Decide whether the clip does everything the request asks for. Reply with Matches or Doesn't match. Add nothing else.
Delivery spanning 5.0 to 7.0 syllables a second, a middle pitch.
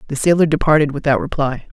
Matches